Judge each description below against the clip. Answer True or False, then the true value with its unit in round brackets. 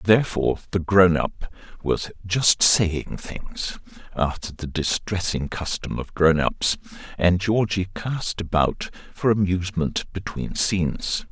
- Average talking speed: False (120 wpm)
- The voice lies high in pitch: False (90 Hz)